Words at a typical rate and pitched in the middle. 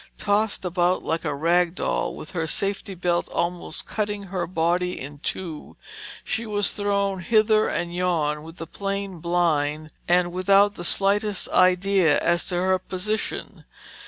Yes: average, 150 wpm; medium, 180 Hz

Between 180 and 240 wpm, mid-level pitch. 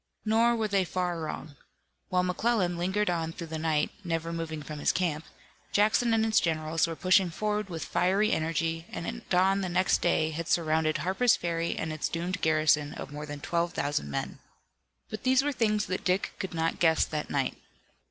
Yes: average, 190 wpm; medium, 170 Hz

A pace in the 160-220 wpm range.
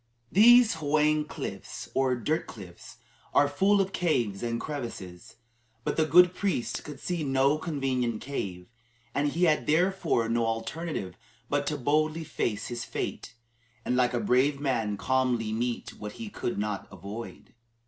No: average, 150 wpm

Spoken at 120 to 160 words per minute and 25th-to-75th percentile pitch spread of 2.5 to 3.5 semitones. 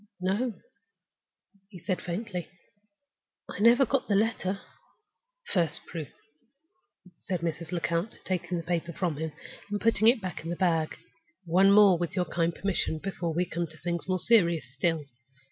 Yes: average, 155 wpm; average, 2.9 semitones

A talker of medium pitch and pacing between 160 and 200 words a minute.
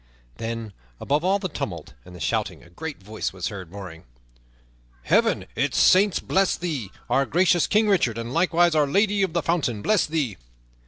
Yes: medium, 150 Hz; average, 175 wpm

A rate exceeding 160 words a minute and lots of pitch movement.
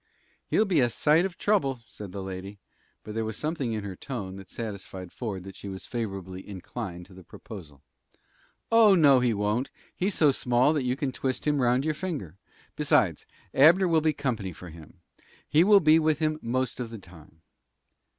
Yes: average, 190 wpm; wide, 7.8 semitones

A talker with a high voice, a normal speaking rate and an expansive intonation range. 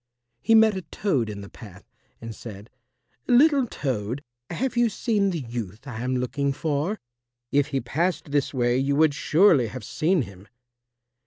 No: medium, 140 Hz; average, 165 wpm; wide, 7.7 semitones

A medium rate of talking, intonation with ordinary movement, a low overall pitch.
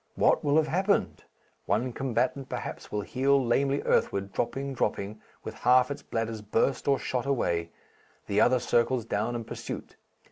Yes: average, 155 wpm; average, 4.2 semitones; low, 125 Hz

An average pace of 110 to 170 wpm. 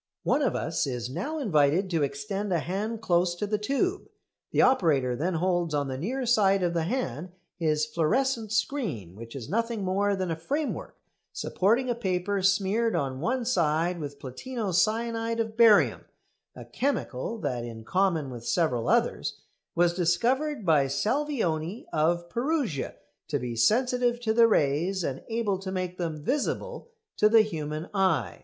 Yes: average, 160 wpm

